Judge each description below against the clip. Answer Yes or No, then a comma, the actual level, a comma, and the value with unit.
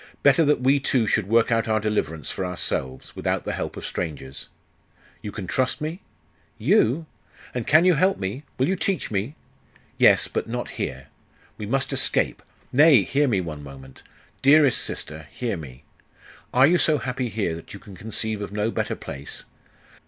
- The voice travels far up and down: Yes, wide, 7.0 semitones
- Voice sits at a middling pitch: No, low, 110 Hz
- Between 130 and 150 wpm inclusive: No, average, 175 wpm